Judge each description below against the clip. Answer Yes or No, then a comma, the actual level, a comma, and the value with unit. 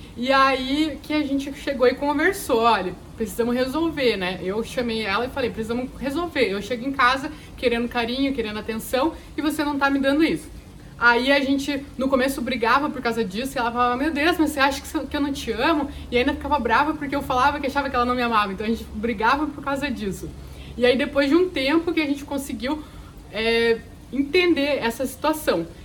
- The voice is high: Yes, very high, 270 Hz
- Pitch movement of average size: Yes, average, 3.4 semitones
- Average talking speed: No, fast, 210 wpm